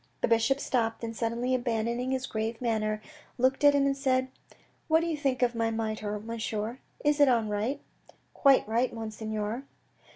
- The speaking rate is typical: Yes, average, 190 wpm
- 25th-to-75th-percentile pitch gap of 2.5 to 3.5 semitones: Yes, average, 3.0 semitones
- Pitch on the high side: Yes, high, 235 Hz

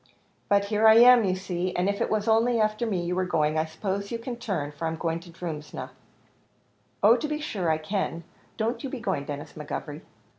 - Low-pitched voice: No, high, 195 Hz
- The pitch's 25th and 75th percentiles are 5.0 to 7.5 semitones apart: Yes, wide, 5.5 semitones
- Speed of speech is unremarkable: No, fast, 220 wpm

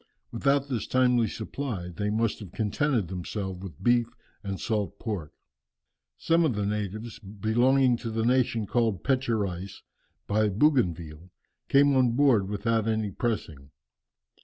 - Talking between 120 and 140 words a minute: Yes, slow, 135 wpm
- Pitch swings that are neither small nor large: Yes, average, 3.9 semitones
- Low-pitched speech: Yes, low, 110 Hz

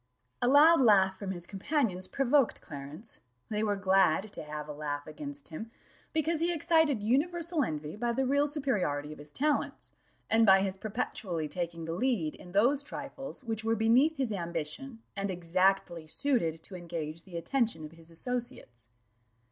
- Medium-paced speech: Yes, average, 165 wpm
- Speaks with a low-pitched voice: No, high, 200 Hz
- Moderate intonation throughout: No, wide, 8.2 semitones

